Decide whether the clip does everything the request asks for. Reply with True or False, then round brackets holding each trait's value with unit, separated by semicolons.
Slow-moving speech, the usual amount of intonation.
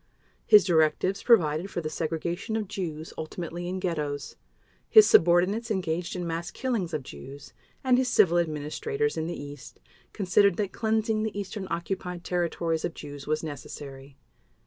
False (150 wpm; 4.6 semitones)